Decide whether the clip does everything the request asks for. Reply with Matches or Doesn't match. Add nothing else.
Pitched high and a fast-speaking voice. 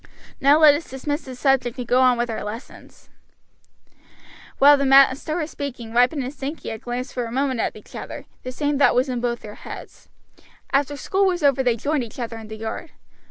Matches